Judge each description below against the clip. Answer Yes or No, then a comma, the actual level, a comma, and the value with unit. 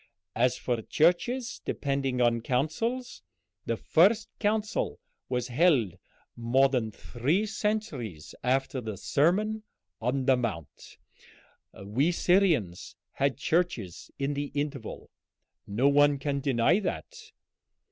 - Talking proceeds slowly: Yes, slow, 110 wpm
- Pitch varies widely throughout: Yes, wide, 6.7 semitones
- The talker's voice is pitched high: No, medium, 140 Hz